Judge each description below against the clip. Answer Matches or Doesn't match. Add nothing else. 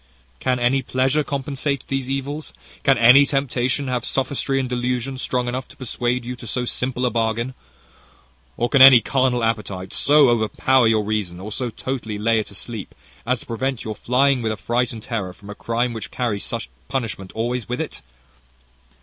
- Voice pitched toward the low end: Matches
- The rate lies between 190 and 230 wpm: Doesn't match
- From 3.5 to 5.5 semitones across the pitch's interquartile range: Doesn't match